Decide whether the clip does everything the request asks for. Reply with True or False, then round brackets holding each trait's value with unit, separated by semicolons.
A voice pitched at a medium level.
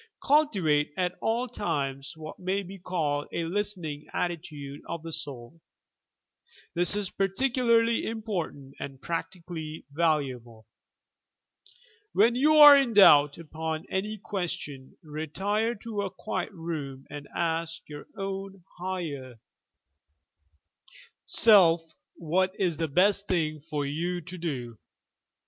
True (170 Hz)